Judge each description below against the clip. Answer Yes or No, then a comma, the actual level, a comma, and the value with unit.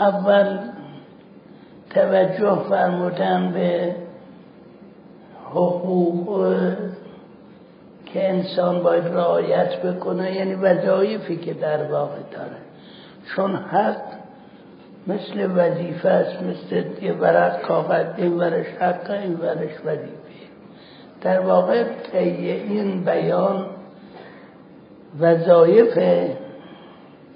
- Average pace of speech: No, slow, 75 wpm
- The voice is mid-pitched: Yes, medium, 180 Hz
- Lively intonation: No, narrow, 1.9 semitones